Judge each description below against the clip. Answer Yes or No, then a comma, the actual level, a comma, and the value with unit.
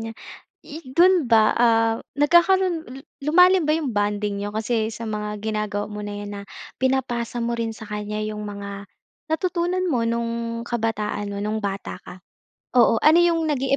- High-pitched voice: Yes, high, 230 Hz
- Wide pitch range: Yes, wide, 5.8 semitones